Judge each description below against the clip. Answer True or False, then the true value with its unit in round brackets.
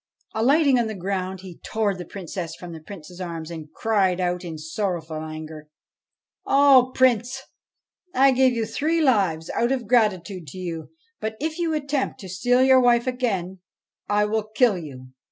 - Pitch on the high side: True (200 Hz)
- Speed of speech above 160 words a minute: True (170 wpm)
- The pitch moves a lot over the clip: True (6.5 semitones)